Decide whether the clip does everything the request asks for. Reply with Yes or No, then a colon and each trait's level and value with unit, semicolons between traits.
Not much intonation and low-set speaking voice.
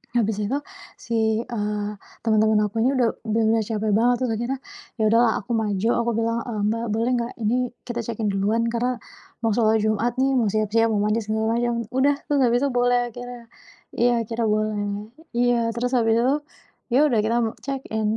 No: narrow, 2.0 semitones; high, 230 Hz